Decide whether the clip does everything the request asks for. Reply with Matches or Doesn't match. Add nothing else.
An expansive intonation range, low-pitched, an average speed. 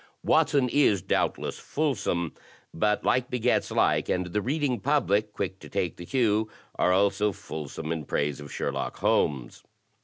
Matches